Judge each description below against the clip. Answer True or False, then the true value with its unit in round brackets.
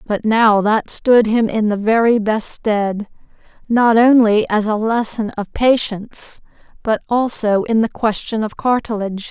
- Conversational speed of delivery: True (155 wpm)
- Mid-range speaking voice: False (220 Hz)